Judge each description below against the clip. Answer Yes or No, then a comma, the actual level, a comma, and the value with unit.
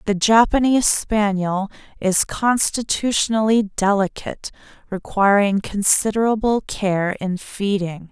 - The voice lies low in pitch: No, high, 205 Hz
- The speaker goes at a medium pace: No, slow, 80 wpm